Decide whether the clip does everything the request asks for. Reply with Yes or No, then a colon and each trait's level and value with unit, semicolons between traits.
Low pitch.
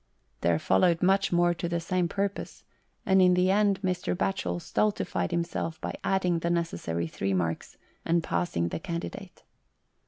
No: medium, 175 Hz